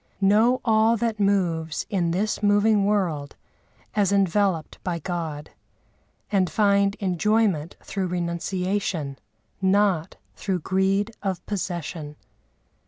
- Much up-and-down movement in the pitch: No, average, 3.1 semitones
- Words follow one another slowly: Yes, slow, 105 wpm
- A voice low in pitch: No, high, 195 Hz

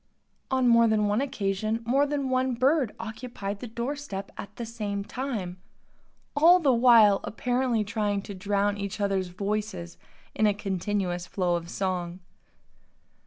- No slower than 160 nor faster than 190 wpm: No, average, 150 wpm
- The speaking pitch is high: Yes, high, 210 Hz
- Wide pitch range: No, average, 3.8 semitones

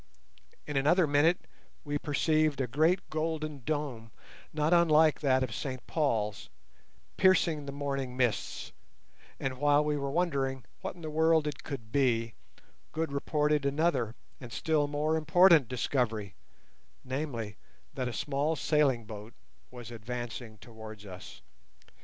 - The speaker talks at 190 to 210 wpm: No, slow, 135 wpm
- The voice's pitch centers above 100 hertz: Yes, medium, 140 Hz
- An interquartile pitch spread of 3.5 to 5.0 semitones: Yes, average, 4.1 semitones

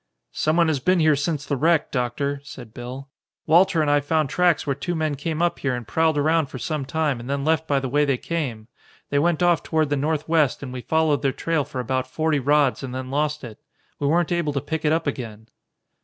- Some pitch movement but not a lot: Yes, average, 3.2 semitones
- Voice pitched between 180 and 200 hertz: No, medium, 145 Hz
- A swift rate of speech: Yes, fast, 230 wpm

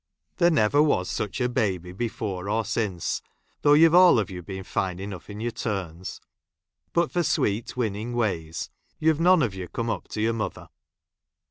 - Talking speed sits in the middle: Yes, average, 175 wpm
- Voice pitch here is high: No, low, 110 Hz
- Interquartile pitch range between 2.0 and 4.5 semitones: No, average, 5.1 semitones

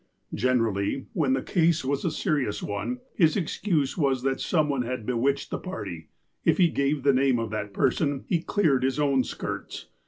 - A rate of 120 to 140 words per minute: No, average, 185 wpm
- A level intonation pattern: No, average, 3.5 semitones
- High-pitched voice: No, low, 135 Hz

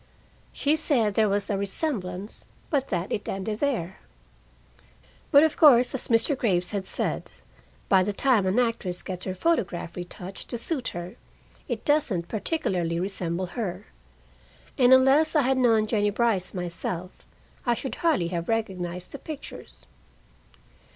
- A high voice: Yes, high, 210 Hz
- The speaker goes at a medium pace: Yes, average, 145 wpm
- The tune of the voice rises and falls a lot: Yes, wide, 6.2 semitones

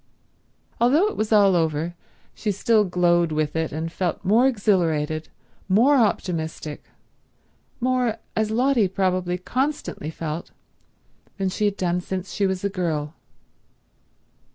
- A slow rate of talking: Yes, slow, 130 wpm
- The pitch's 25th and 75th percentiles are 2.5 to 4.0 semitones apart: No, average, 4.7 semitones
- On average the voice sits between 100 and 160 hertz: No, medium, 185 Hz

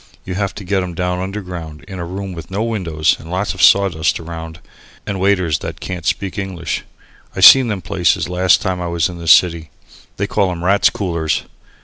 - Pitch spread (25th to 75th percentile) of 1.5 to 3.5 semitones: Yes, narrow, 2.6 semitones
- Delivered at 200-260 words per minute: Yes, fast, 205 wpm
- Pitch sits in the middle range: No, very low, 90 Hz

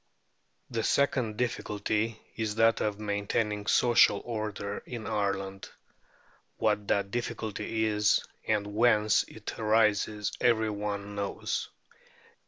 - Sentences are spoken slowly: Yes, slow, 105 wpm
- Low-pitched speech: Yes, low, 105 Hz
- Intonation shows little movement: Yes, narrow, 1.6 semitones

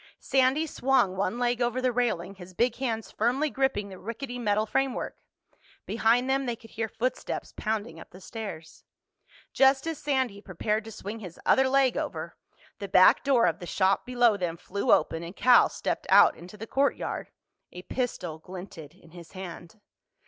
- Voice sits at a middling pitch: No, high, 220 Hz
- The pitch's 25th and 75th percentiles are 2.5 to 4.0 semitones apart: No, wide, 5.4 semitones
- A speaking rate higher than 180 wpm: No, average, 175 wpm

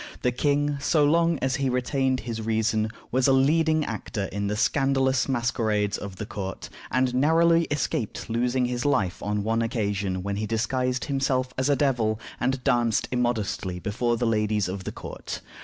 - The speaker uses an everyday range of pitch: Yes, average, 3.9 semitones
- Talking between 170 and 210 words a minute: Yes, average, 175 wpm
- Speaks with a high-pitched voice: No, low, 125 Hz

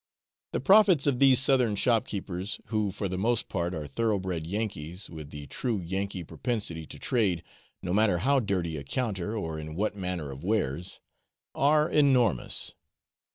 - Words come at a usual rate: Yes, average, 160 wpm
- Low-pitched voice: Yes, low, 100 Hz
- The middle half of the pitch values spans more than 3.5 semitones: Yes, wide, 5.5 semitones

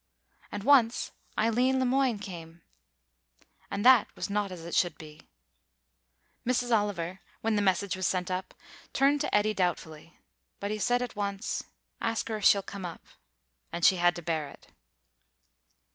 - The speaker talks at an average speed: Yes, average, 160 wpm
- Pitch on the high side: Yes, high, 200 Hz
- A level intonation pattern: No, average, 4.5 semitones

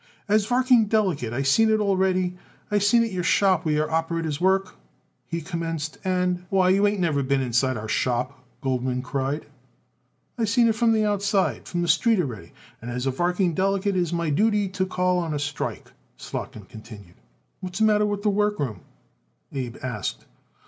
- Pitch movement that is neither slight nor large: No, wide, 6.5 semitones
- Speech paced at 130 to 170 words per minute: No, average, 185 wpm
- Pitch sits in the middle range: Yes, medium, 180 Hz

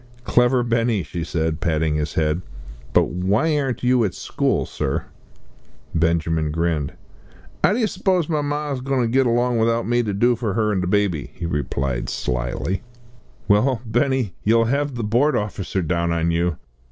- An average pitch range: No, wide, 6.8 semitones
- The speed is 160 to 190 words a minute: Yes, average, 165 wpm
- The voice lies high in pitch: No, low, 105 Hz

